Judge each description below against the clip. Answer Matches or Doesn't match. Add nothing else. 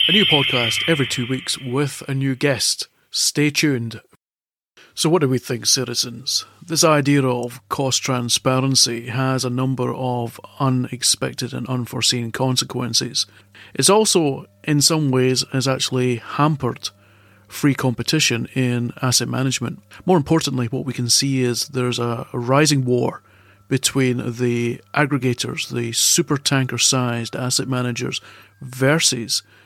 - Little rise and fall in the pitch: Matches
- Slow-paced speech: Matches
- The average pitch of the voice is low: Matches